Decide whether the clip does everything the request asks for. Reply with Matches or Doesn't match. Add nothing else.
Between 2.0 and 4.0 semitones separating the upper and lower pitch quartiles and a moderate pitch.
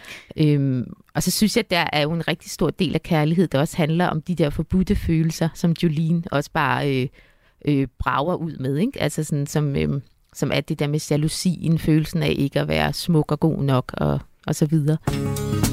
Matches